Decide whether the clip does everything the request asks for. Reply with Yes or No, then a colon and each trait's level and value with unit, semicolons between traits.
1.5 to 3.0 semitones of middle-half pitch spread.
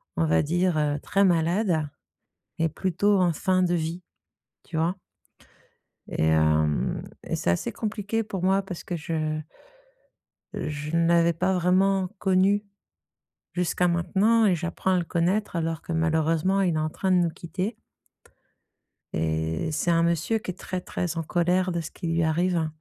Yes: average, 2.7 semitones